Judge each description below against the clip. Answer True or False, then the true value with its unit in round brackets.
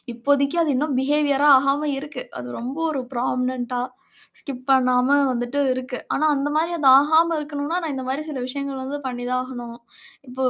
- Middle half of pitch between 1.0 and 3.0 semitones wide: True (2.5 semitones)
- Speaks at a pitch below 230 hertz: False (275 Hz)